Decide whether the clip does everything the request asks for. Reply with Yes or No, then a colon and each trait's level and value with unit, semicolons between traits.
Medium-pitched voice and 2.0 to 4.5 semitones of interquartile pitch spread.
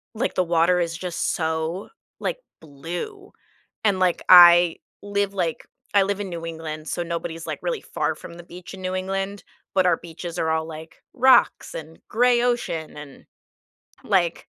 Yes: medium, 175 Hz; average, 3.1 semitones